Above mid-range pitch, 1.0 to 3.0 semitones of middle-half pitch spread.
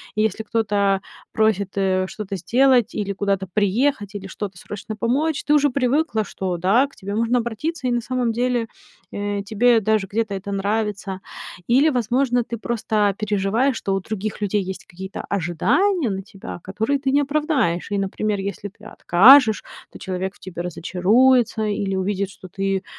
No: high, 210 Hz; average, 3.8 semitones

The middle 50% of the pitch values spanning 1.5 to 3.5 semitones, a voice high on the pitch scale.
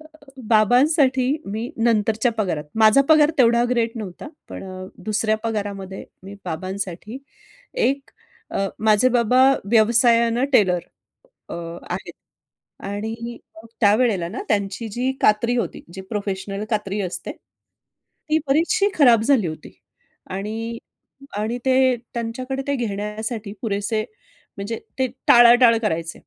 Yes: average, 3.2 semitones; high, 225 Hz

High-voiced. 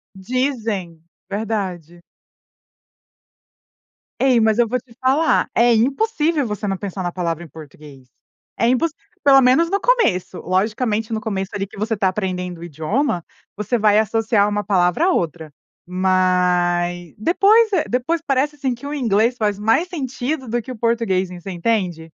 Yes: high, 215 Hz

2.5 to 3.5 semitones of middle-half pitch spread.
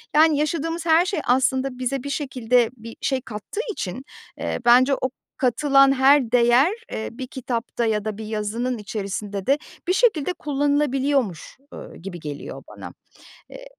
No: average, 4.3 semitones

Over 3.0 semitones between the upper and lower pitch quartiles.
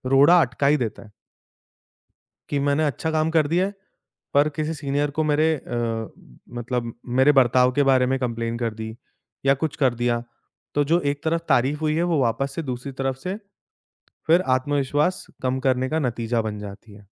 Yes: average, 4.1 semitones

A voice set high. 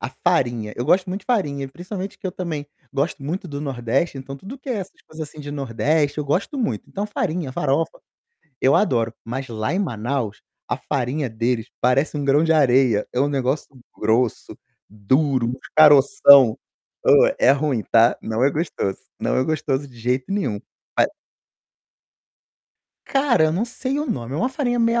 No: medium, 140 Hz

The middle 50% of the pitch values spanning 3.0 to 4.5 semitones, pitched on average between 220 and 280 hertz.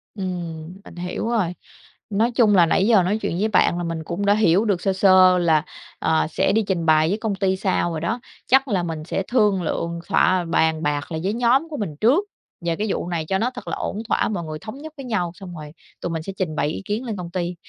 No: average, 4.2 semitones; medium, 185 Hz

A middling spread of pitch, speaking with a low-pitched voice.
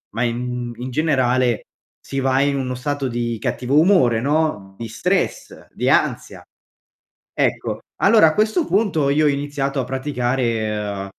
Yes: average, 3.5 semitones; low, 130 Hz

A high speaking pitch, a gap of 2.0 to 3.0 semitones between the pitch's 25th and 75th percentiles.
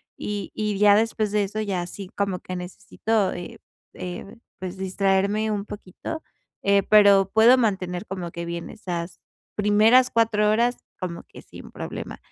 Yes: high, 200 Hz; narrow, 2.6 semitones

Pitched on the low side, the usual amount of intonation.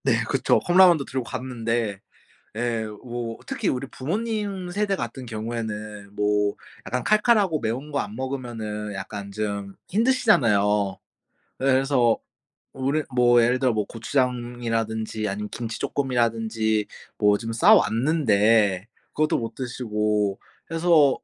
Yes: low, 120 Hz; average, 4.4 semitones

